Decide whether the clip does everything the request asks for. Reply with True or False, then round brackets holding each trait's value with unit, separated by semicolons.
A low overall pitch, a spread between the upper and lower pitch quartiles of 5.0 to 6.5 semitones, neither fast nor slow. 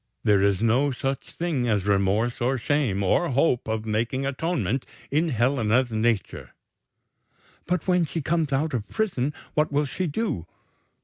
True (130 Hz; 5.4 semitones; 150 wpm)